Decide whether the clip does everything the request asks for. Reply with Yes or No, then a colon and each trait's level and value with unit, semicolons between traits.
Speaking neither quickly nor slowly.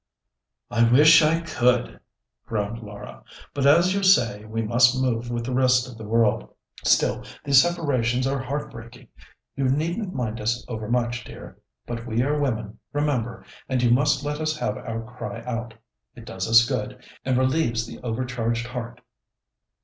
Yes: average, 165 wpm